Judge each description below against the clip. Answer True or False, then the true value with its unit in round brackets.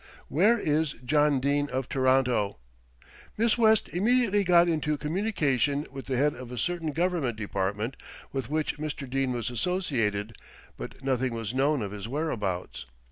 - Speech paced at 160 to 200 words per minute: False (150 wpm)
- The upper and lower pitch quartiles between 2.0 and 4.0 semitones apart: False (4.9 semitones)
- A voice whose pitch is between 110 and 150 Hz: True (140 Hz)